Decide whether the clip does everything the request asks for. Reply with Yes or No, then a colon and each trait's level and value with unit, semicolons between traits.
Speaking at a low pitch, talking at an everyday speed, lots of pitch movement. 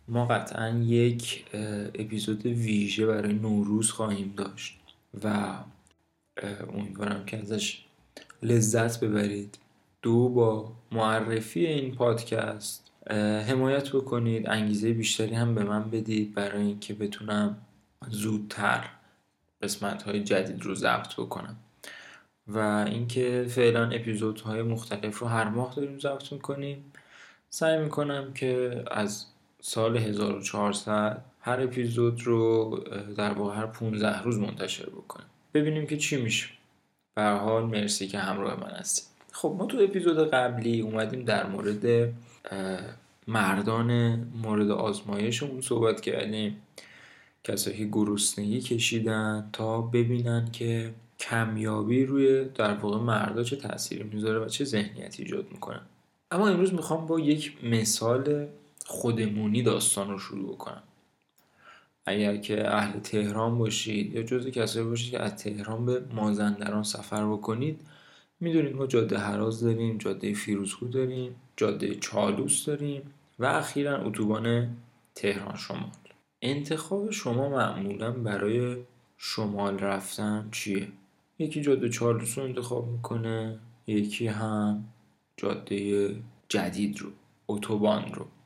No: low, 110 Hz; average, 120 wpm; narrow, 2.5 semitones